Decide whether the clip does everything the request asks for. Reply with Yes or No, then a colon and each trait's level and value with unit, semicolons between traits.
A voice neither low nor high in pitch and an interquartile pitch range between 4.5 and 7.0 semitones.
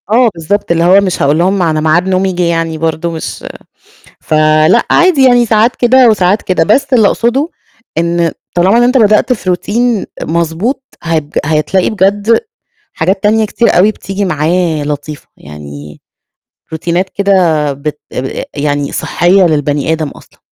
Yes: medium, 180 Hz; average, 5.1 semitones